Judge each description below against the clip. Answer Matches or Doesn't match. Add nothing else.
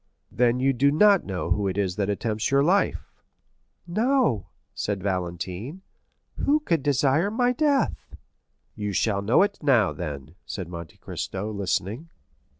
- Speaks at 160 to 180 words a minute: Doesn't match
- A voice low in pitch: Matches